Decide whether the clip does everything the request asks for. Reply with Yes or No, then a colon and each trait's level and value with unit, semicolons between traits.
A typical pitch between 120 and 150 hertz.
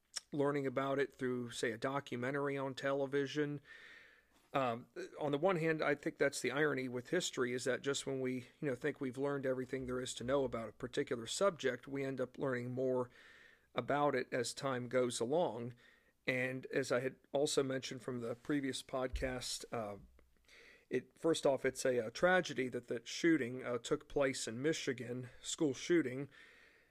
Yes: low, 135 Hz